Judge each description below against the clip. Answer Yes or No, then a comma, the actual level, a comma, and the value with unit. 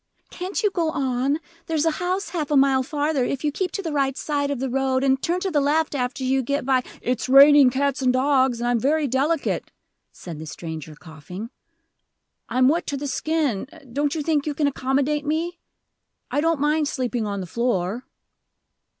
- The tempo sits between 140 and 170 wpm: No, average, 200 wpm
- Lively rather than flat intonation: No, average, 3.1 semitones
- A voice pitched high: Yes, very high, 275 Hz